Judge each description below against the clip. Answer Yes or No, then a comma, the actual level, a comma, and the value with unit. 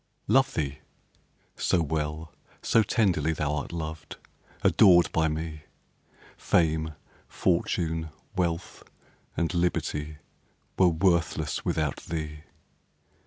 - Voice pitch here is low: Yes, very low, 80 Hz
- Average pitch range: No, narrow, 2.0 semitones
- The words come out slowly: Yes, slow, 90 wpm